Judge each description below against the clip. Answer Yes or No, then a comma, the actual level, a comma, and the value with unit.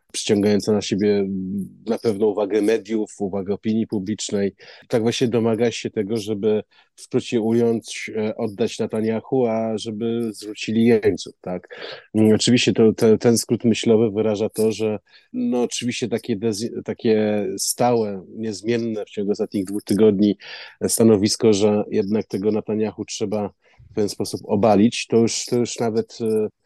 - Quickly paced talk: No, average, 135 wpm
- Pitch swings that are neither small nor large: No, narrow, 1.4 semitones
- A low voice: Yes, low, 110 Hz